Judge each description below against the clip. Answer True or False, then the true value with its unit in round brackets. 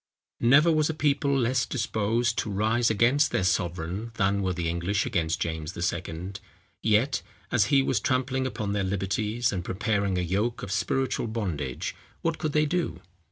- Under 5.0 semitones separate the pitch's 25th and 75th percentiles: False (5.6 semitones)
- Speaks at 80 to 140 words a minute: False (165 wpm)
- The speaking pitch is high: False (110 Hz)